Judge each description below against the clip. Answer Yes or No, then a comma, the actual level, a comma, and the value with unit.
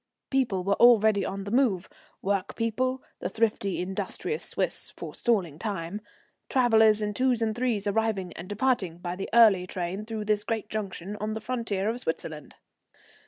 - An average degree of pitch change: Yes, average, 3.1 semitones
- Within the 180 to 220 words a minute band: No, average, 160 wpm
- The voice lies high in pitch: Yes, high, 210 Hz